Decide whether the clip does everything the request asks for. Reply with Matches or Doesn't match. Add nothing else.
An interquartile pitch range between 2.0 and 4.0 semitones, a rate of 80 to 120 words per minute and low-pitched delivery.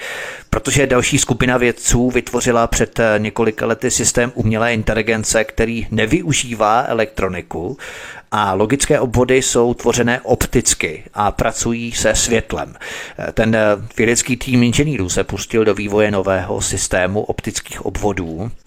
Matches